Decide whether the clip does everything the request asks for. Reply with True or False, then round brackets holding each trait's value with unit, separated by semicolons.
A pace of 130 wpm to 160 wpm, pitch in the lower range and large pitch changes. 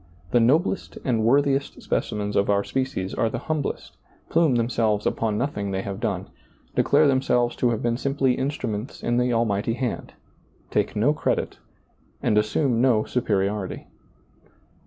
False (150 wpm; 120 Hz; 4.2 semitones)